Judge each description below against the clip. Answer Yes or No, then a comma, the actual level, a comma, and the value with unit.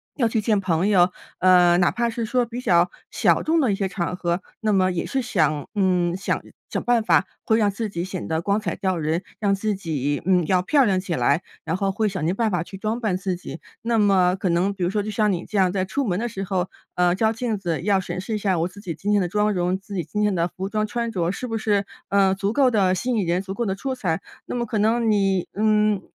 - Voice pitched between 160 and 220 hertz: Yes, high, 195 Hz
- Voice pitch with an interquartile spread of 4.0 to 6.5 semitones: No, average, 3.1 semitones